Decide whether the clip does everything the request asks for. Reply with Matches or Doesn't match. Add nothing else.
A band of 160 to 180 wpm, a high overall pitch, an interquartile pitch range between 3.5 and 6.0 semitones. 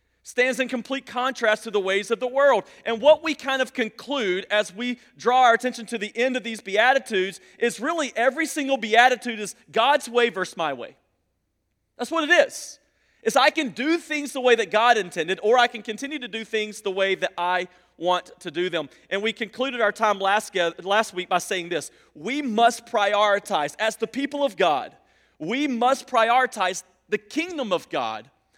Doesn't match